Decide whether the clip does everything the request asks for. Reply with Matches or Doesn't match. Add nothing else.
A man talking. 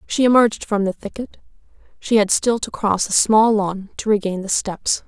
Doesn't match